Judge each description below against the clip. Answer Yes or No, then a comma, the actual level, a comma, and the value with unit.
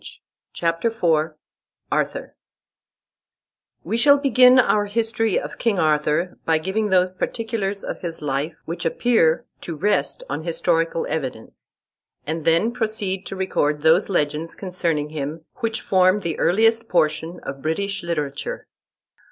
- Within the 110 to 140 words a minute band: Yes, slow, 135 wpm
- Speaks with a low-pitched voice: No, medium, 175 Hz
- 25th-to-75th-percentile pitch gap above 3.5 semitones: Yes, average, 4.9 semitones